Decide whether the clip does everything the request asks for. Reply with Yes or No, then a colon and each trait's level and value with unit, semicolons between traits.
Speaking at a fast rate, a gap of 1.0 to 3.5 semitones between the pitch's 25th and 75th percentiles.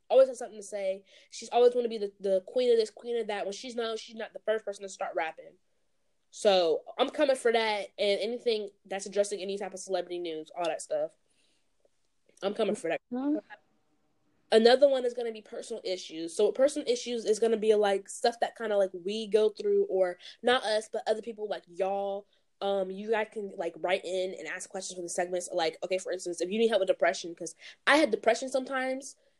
No: fast, 225 wpm; average, 3.9 semitones